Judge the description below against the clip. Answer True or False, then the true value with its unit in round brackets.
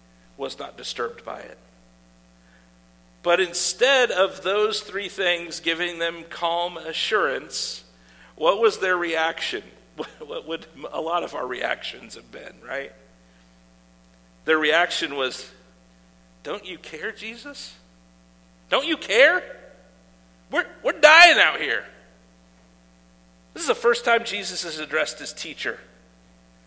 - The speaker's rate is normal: False (120 wpm)